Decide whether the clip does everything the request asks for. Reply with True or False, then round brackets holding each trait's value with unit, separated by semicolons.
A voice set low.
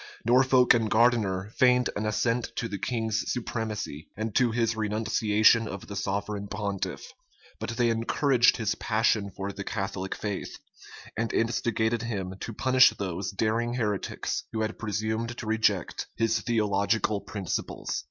True (110 Hz)